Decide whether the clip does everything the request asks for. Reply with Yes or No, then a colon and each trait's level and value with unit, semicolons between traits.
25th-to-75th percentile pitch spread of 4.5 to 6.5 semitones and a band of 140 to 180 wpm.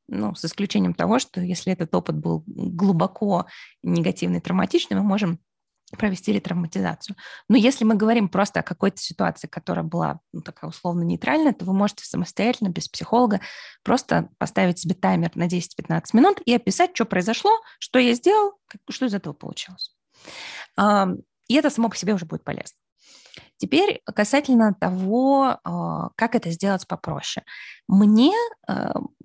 Yes: average, 5.2 semitones; average, 145 wpm